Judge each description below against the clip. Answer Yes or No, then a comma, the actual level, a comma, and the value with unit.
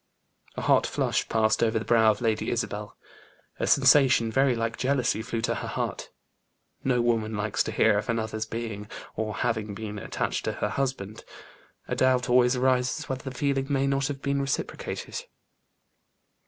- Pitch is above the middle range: No, low, 120 Hz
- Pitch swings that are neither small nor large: Yes, average, 3.1 semitones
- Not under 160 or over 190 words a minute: Yes, average, 170 wpm